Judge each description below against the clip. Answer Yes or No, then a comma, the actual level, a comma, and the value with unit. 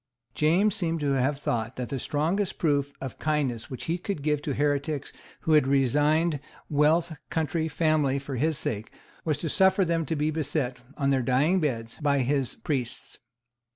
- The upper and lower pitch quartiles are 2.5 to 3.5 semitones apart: Yes, average, 2.9 semitones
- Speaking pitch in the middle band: Yes, medium, 145 Hz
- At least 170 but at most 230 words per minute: Yes, average, 175 wpm